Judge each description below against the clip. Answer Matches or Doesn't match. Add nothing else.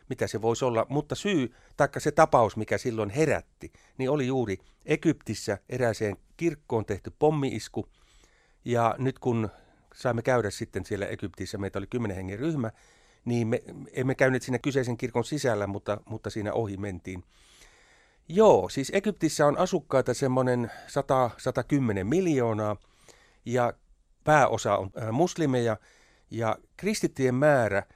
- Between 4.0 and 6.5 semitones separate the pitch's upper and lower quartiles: Matches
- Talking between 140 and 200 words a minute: Doesn't match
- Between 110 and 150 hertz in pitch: Matches